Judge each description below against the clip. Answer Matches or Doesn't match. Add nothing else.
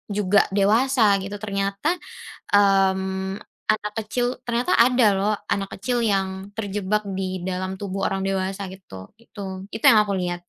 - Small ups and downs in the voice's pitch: Matches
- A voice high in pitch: Matches